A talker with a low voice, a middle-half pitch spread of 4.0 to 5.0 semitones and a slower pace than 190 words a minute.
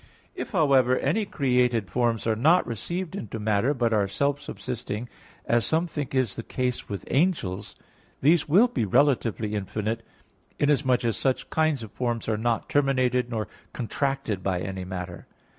Yes: low, 125 Hz; average, 4.6 semitones; average, 160 wpm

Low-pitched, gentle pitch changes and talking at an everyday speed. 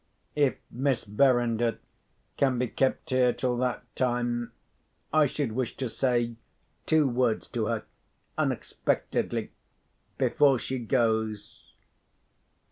No: low, 125 Hz; narrow, 2.0 semitones; slow, 100 wpm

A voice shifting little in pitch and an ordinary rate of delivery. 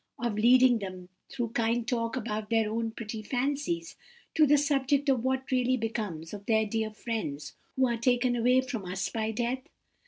No: average, 3.0 semitones; average, 180 wpm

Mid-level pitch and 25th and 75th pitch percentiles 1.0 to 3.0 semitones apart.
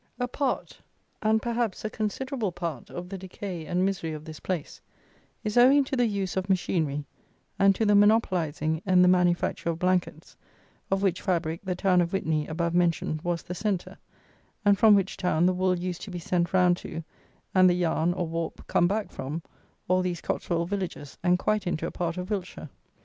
Yes: medium, 180 Hz; average, 2.7 semitones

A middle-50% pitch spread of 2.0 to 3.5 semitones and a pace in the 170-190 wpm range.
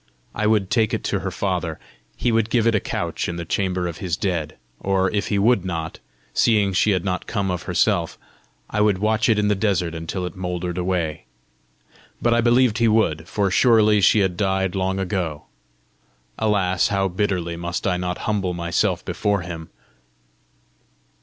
Yes: average, 3.1 semitones; average, 180 wpm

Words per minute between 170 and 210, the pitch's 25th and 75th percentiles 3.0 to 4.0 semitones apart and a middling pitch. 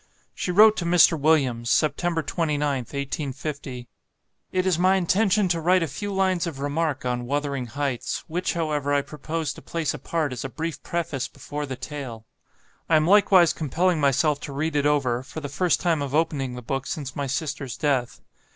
Yes: average, 185 wpm; average, 3.5 semitones; medium, 150 Hz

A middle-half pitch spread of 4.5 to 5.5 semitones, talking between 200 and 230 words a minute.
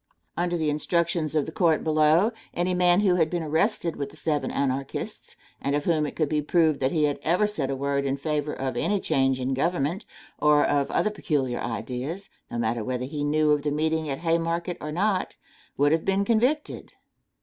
No: average, 3.7 semitones; fast, 205 wpm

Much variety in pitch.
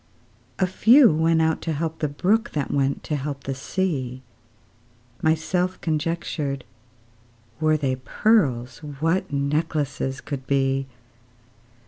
No: average, 3.2 semitones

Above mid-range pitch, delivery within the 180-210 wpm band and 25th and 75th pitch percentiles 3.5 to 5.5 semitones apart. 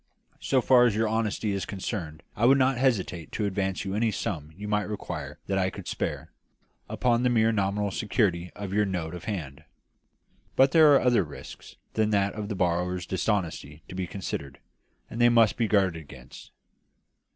No: low, 100 Hz; average, 185 wpm; average, 4.0 semitones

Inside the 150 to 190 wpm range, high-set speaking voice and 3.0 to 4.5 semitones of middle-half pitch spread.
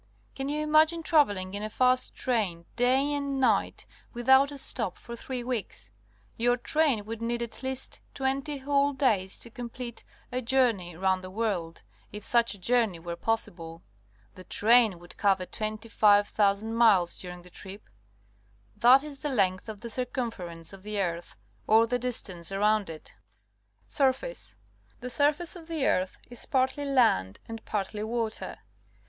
No: average, 160 wpm; high, 230 Hz; average, 5.1 semitones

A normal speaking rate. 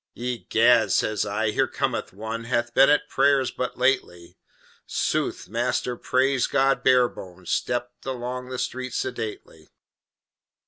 No: slow, 130 wpm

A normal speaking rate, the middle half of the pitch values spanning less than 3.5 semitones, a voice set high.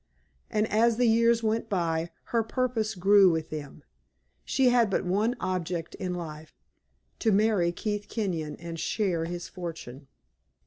No: average, 145 wpm; average, 4.8 semitones; high, 195 Hz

